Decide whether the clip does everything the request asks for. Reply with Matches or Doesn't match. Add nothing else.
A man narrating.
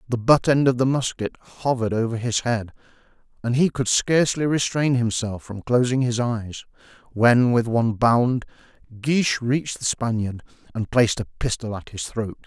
Matches